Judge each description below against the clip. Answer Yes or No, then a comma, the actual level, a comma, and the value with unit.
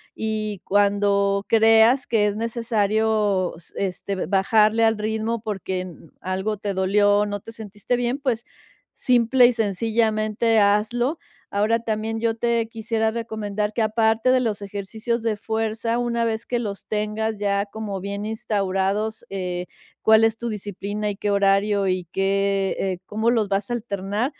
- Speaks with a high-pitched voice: Yes, high, 215 Hz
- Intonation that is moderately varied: No, narrow, 2.1 semitones